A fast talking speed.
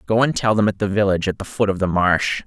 Yes: fast, 315 wpm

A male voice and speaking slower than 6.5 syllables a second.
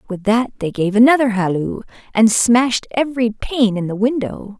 No: female; 4.9 syllables/s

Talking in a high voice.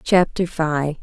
No: medium, 160 Hz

